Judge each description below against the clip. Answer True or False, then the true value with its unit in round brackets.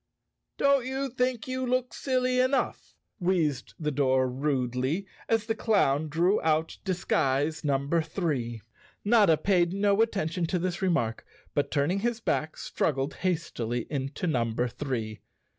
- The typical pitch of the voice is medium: True (165 Hz)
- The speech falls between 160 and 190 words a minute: False (140 wpm)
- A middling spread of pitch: False (7.3 semitones)